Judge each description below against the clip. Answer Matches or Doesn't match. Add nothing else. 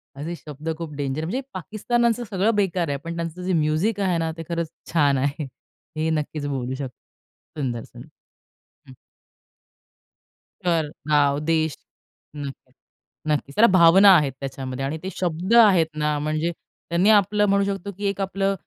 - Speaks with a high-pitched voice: Doesn't match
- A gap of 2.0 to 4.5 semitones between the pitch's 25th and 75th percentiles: Doesn't match